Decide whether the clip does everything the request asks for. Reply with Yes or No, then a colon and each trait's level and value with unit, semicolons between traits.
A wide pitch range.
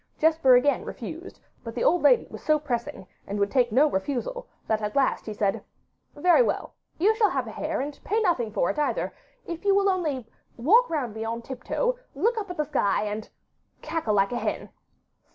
Yes: wide, 7.8 semitones